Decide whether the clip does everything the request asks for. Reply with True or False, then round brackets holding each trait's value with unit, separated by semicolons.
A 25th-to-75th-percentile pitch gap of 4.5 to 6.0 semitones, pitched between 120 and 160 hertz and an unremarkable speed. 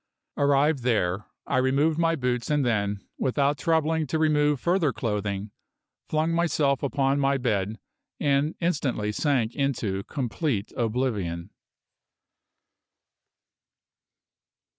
False (5.3 semitones; 135 Hz; 100 wpm)